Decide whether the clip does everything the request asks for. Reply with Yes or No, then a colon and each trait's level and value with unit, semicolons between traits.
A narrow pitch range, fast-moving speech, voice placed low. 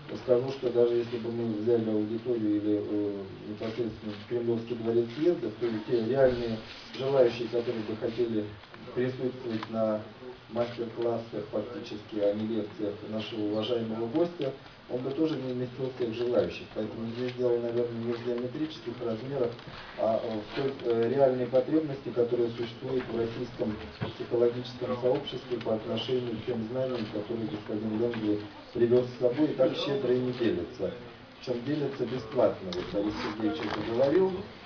No: narrow, 2.2 semitones; average, 145 wpm; low, 120 Hz